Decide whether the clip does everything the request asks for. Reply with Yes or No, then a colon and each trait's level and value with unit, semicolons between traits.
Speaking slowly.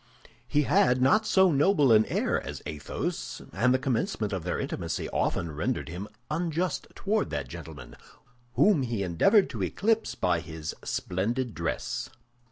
No: average, 150 wpm